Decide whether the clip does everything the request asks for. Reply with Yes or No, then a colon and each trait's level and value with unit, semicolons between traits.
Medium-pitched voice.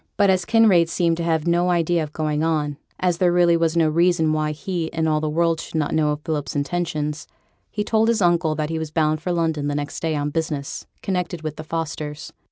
Yes: medium, 160 Hz